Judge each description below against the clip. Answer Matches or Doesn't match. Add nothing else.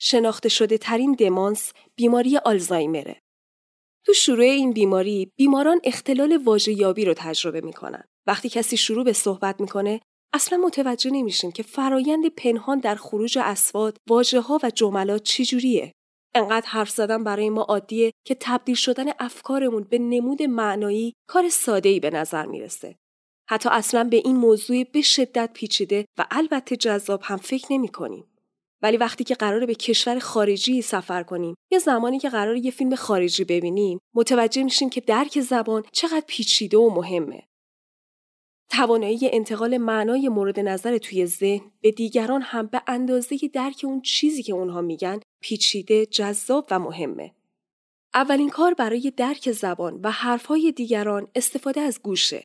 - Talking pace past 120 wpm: Matches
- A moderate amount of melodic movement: Matches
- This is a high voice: Matches